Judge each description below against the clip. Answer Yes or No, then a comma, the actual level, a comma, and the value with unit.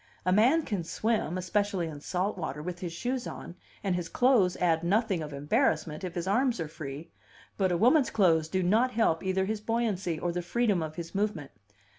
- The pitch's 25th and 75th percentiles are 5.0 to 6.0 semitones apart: No, average, 4.6 semitones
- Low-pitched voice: No, medium, 185 Hz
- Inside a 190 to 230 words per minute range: Yes, average, 200 wpm